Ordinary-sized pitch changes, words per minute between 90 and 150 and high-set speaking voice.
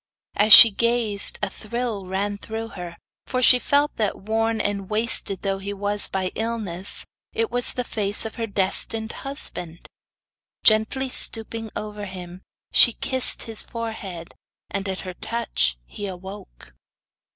Yes: average, 3.0 semitones; average, 145 wpm; high, 210 Hz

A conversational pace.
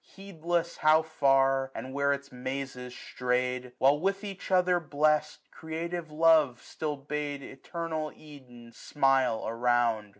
No: slow, 130 wpm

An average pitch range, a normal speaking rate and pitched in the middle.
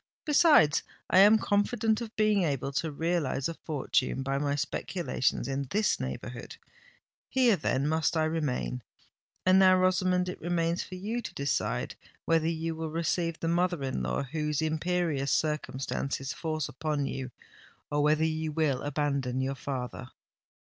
Yes: average, 4.5 semitones; average, 150 wpm; medium, 160 Hz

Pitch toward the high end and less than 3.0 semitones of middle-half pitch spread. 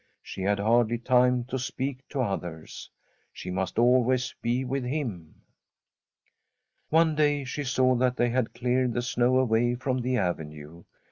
No: low, 125 Hz; narrow, 2.5 semitones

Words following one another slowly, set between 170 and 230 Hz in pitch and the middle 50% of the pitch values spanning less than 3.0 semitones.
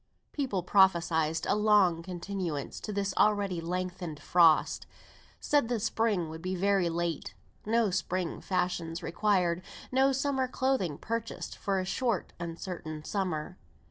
No: slow, 130 wpm; medium, 185 Hz; average, 3.7 semitones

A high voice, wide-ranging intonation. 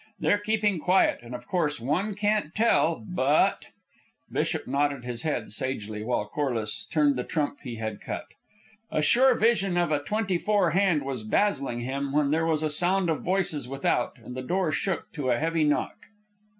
No: medium, 150 Hz; wide, 6.3 semitones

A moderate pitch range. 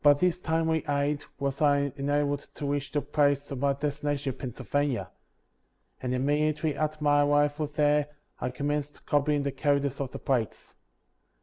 No: narrow, 1.0 semitones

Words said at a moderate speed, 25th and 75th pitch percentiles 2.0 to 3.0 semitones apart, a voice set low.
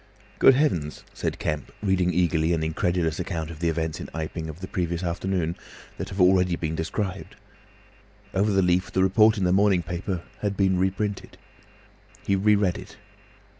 Yes: average, 170 wpm; average, 2.7 semitones; very low, 90 Hz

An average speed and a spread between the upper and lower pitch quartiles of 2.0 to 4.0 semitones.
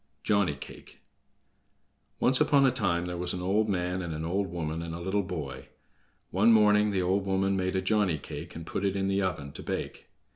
No: fast, 210 wpm; average, 2.8 semitones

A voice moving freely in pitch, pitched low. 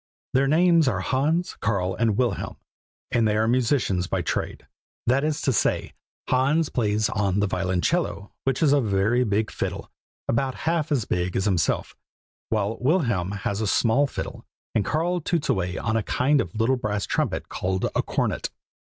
Yes: wide, 5.8 semitones; low, 115 Hz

